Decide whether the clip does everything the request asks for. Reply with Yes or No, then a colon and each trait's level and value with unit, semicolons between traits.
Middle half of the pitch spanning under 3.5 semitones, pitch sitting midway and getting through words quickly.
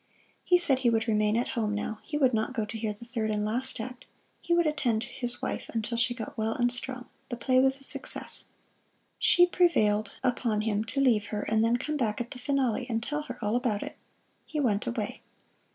No: average, 3.1 semitones; high, 240 Hz; fast, 220 wpm